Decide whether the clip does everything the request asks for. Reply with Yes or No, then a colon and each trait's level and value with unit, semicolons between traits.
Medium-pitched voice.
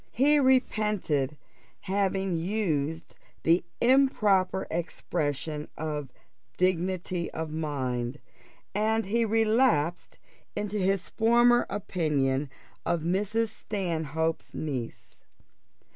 Yes: medium, 180 Hz